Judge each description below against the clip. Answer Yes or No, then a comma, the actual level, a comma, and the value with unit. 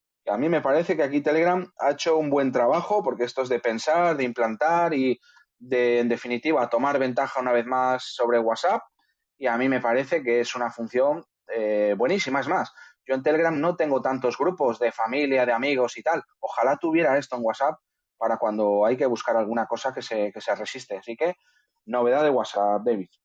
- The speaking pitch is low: Yes, low, 125 Hz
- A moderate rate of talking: No, fast, 205 wpm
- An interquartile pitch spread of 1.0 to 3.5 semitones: No, average, 3.9 semitones